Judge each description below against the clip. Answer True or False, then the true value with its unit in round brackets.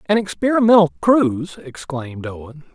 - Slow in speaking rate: True (110 wpm)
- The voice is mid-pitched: True (170 Hz)